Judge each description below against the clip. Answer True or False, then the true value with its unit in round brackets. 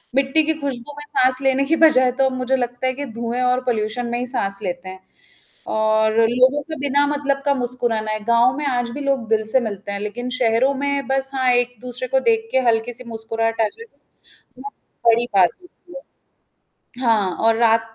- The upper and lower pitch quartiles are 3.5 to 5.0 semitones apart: False (3.1 semitones)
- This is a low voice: False (245 Hz)